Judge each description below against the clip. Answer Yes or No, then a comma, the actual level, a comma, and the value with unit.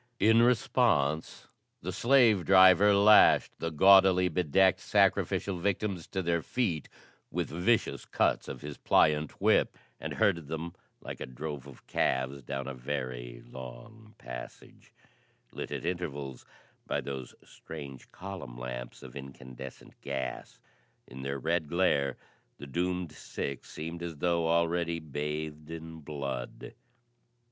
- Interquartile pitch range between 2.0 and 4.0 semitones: No, average, 5.0 semitones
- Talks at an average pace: No, slow, 130 wpm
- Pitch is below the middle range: Yes, very low, 80 Hz